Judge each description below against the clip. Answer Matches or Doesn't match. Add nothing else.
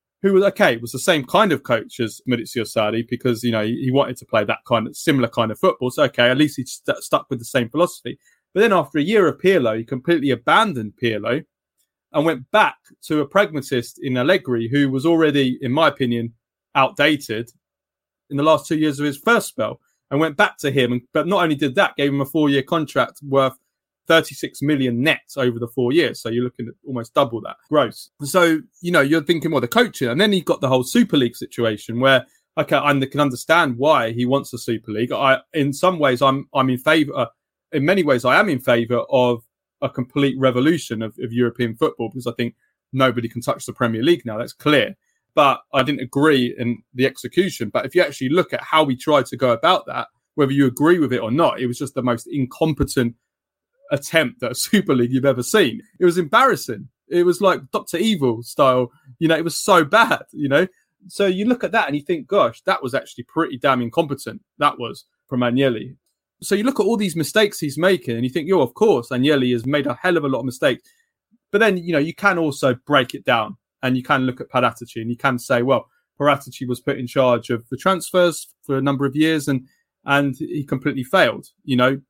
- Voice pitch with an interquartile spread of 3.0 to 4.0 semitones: Doesn't match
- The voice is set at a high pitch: Doesn't match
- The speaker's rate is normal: Doesn't match